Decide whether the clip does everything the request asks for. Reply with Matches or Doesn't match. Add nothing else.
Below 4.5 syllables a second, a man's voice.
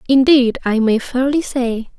Doesn't match